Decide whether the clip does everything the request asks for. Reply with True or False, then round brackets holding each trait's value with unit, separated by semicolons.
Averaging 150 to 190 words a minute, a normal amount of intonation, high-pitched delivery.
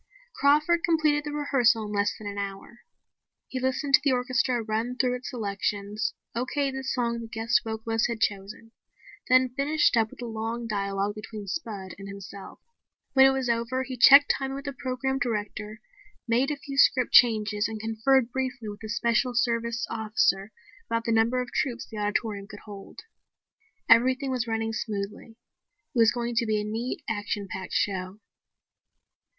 True (170 wpm; 3.4 semitones; 230 Hz)